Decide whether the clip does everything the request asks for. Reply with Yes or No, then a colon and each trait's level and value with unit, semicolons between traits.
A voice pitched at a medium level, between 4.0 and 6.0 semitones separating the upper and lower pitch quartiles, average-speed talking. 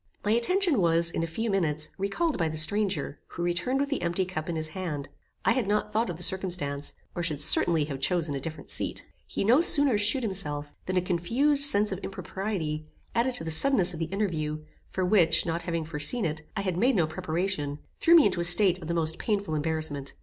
No: medium, 175 Hz; average, 4.9 semitones; fast, 220 wpm